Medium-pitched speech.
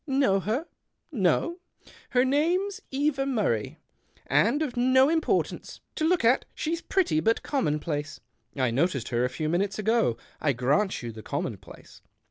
No: high, 220 Hz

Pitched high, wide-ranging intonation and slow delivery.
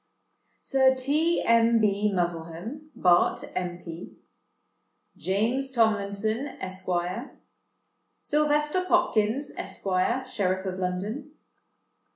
Yes: high, 220 Hz; wide, 6.4 semitones; slow, 80 wpm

